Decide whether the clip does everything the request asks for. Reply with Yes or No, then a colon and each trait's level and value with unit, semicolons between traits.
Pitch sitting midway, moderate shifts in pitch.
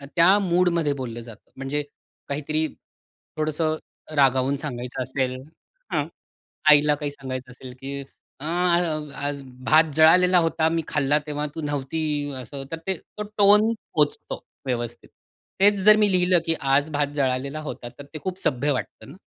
Yes: medium, 145 Hz; average, 3.4 semitones